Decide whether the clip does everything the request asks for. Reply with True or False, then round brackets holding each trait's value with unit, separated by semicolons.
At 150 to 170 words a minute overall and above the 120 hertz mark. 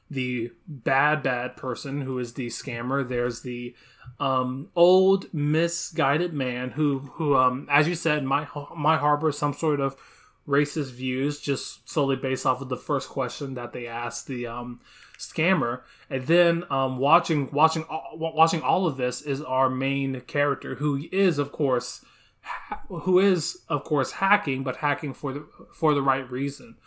True (165 wpm; 140 Hz)